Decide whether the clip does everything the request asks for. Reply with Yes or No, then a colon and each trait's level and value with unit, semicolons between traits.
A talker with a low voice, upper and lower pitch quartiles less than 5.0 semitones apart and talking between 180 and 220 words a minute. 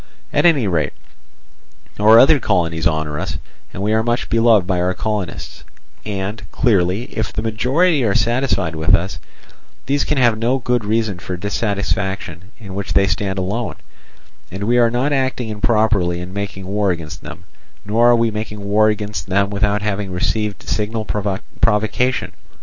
No: low, 105 Hz; average, 3.2 semitones; average, 165 wpm